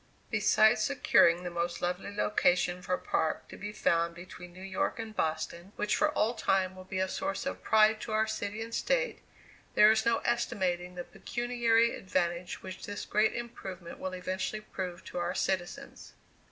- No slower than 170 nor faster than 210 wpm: Yes, average, 180 wpm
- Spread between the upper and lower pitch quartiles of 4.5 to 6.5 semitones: No, average, 3.6 semitones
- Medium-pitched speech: No, high, 195 Hz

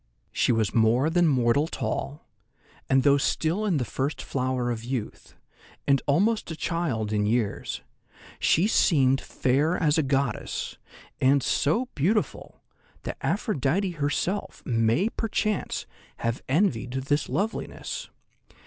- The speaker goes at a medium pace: No, slow, 125 wpm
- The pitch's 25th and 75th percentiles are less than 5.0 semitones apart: No, wide, 5.6 semitones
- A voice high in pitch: No, medium, 140 Hz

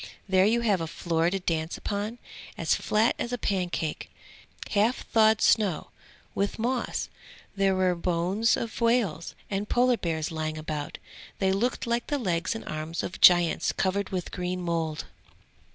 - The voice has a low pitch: No, high, 190 Hz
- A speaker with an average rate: Yes, average, 155 wpm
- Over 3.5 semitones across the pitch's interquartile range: Yes, average, 4.7 semitones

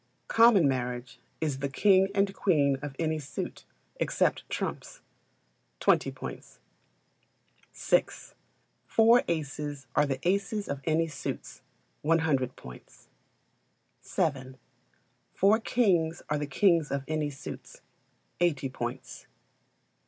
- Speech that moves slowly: Yes, slow, 110 wpm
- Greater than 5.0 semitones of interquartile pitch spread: Yes, wide, 5.4 semitones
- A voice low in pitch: No, medium, 155 Hz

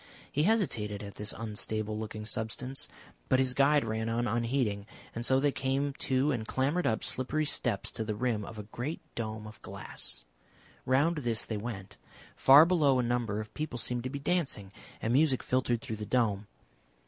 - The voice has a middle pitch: No, low, 120 Hz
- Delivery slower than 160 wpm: No, average, 185 wpm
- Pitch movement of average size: Yes, average, 4.0 semitones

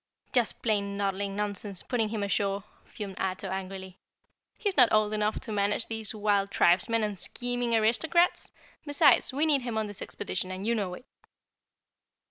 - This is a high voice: Yes, high, 210 Hz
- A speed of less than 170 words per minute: Yes, average, 160 wpm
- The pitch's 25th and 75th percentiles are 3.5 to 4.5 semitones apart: No, average, 2.8 semitones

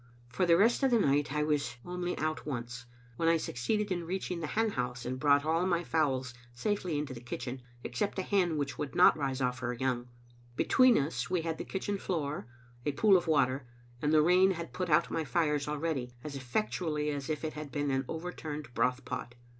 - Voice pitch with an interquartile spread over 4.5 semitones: Yes, average, 4.9 semitones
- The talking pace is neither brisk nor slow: No, fast, 210 wpm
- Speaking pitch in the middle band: Yes, medium, 150 Hz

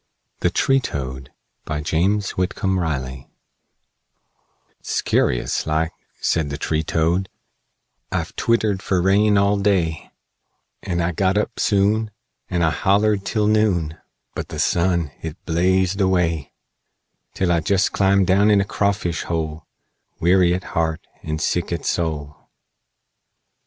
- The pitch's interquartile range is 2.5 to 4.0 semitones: Yes, average, 3.6 semitones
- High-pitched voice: No, very low, 90 Hz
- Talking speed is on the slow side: Yes, slow, 130 wpm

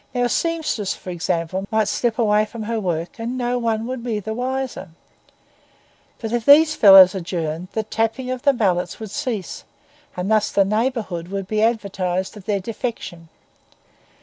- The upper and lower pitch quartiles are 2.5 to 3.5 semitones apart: No, average, 4.2 semitones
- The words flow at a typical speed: Yes, average, 160 wpm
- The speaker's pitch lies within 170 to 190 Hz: No, high, 215 Hz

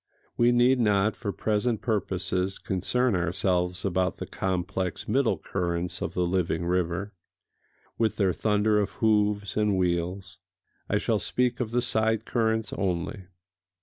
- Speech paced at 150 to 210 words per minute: No, average, 140 wpm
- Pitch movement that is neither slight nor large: Yes, average, 3.5 semitones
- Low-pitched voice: Yes, low, 100 Hz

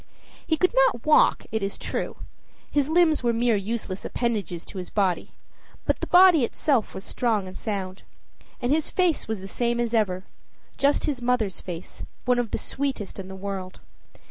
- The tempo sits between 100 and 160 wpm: No, average, 180 wpm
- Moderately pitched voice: No, high, 230 Hz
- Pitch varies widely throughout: Yes, wide, 6.4 semitones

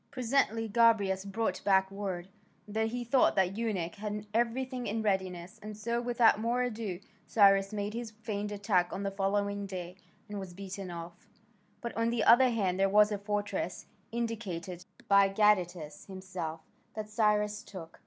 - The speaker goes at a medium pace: Yes, average, 160 wpm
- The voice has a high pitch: Yes, high, 205 Hz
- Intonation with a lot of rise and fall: No, average, 2.9 semitones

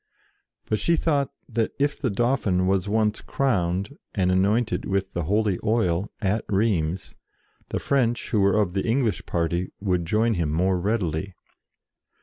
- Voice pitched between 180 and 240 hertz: No, low, 100 Hz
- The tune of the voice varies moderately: Yes, average, 3.9 semitones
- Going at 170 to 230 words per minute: No, average, 150 wpm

